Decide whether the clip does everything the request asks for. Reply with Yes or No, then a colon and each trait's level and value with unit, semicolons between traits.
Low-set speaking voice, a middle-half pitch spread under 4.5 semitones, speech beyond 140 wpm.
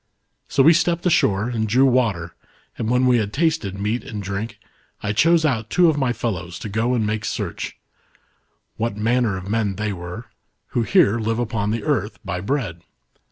Yes: low, 115 Hz; average, 3.8 semitones; average, 185 wpm